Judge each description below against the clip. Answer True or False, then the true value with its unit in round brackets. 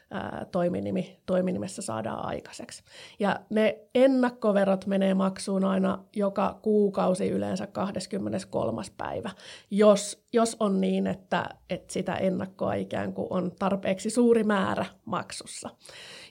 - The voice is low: False (195 Hz)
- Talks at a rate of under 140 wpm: True (105 wpm)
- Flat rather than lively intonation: True (2.3 semitones)